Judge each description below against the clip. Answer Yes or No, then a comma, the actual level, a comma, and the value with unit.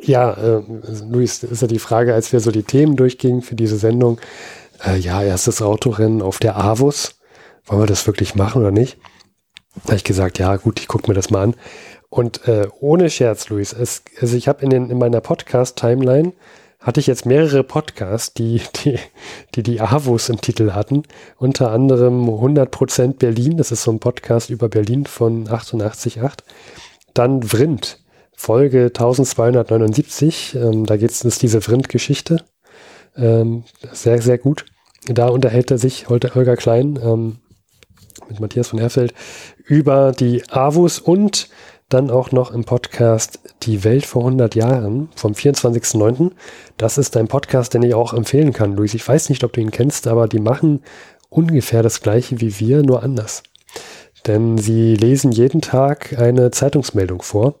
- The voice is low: Yes, low, 120 Hz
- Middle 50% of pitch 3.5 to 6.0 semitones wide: No, average, 2.9 semitones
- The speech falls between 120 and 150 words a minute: No, average, 165 wpm